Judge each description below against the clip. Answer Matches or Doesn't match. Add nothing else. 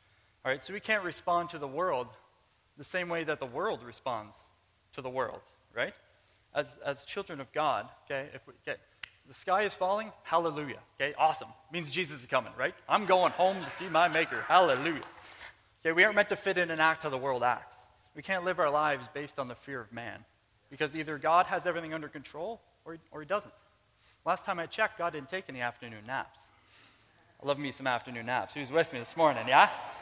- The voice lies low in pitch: Doesn't match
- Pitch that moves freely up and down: Matches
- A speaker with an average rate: Doesn't match